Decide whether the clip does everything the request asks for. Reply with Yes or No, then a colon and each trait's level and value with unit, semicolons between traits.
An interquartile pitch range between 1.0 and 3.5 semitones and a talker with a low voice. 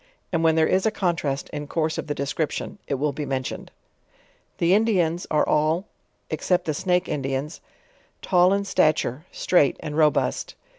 No: average, 3.2 semitones; medium, 160 Hz